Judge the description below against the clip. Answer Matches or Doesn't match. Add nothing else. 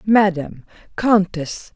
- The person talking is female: Matches